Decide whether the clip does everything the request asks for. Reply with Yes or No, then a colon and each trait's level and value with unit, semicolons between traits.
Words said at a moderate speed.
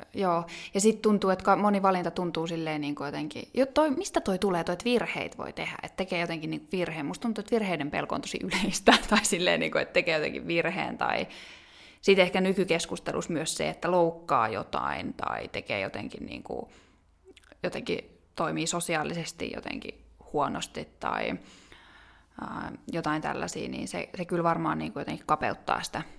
No: fast, 170 wpm